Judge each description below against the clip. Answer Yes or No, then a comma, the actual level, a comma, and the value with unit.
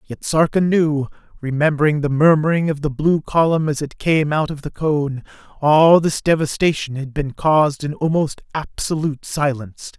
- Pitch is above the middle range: No, medium, 150 Hz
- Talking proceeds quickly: No, average, 160 wpm